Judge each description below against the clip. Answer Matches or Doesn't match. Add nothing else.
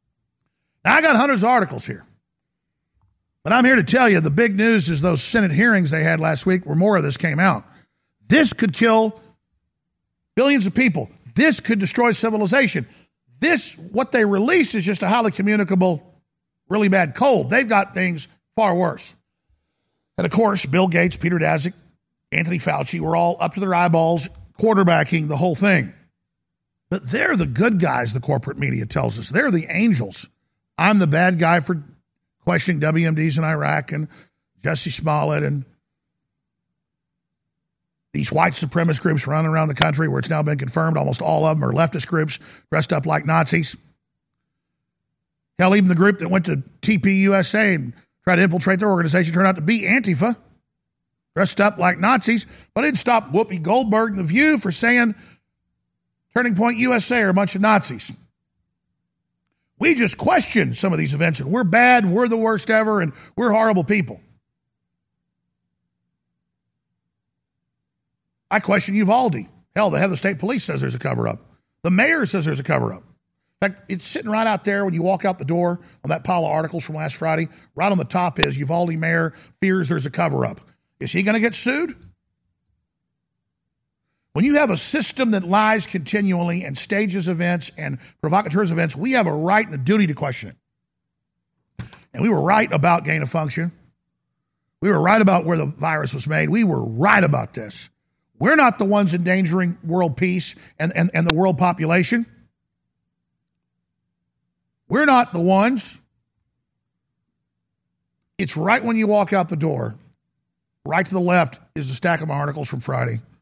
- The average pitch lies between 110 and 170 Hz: Doesn't match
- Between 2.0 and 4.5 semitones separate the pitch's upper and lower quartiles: Doesn't match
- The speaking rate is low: Doesn't match